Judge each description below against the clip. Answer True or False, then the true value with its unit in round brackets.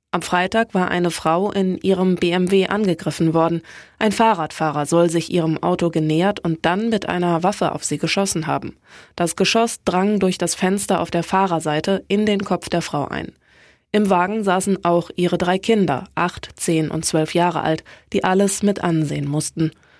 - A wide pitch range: False (2.9 semitones)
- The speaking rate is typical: True (175 wpm)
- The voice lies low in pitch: False (175 Hz)